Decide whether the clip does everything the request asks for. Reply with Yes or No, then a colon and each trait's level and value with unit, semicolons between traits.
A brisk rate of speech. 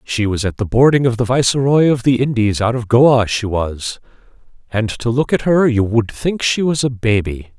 Yes: fast, 220 wpm